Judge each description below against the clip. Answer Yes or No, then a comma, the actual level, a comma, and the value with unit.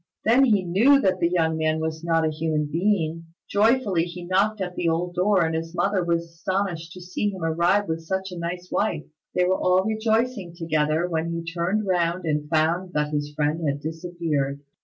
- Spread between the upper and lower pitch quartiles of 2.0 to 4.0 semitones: Yes, average, 2.7 semitones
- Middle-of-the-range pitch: Yes, medium, 170 Hz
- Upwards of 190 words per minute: Yes, average, 200 wpm